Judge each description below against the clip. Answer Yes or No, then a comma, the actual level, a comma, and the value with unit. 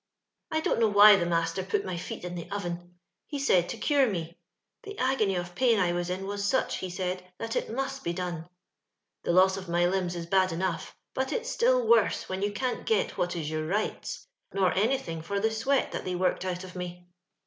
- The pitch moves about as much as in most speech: Yes, average, 4.2 semitones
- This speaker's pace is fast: Yes, fast, 220 wpm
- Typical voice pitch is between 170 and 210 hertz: Yes, medium, 185 Hz